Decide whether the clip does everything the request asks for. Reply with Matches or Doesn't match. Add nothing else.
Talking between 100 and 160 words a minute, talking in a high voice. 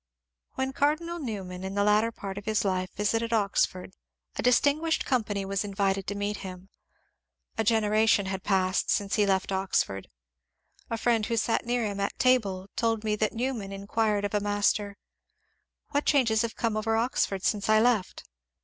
Doesn't match